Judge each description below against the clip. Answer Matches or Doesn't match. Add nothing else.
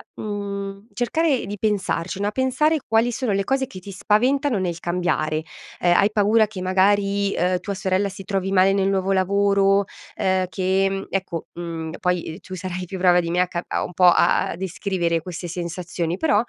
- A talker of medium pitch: Doesn't match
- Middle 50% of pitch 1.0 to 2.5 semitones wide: Matches